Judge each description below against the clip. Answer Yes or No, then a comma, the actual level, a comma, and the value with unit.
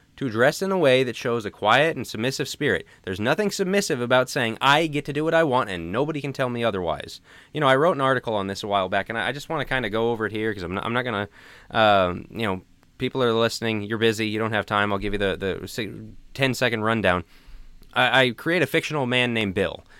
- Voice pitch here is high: No, low, 120 Hz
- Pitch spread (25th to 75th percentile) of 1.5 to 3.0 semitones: No, average, 4.1 semitones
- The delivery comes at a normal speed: No, fast, 260 wpm